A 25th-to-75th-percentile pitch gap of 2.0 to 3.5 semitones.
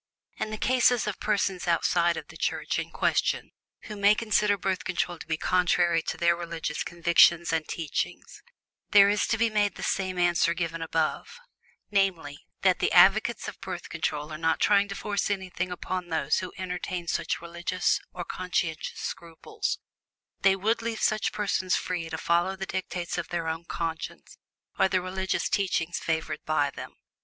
Yes: average, 2.9 semitones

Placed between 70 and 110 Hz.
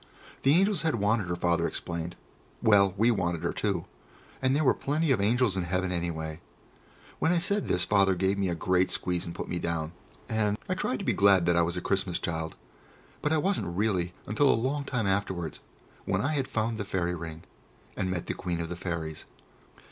Yes: very low, 95 Hz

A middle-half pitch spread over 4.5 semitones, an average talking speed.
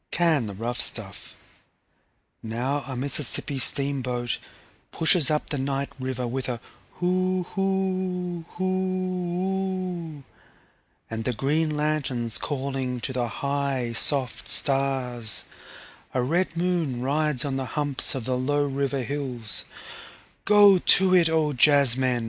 No: average, 5.2 semitones; slow, 125 wpm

